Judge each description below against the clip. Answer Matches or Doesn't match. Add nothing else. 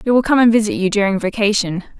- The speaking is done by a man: Doesn't match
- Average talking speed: Doesn't match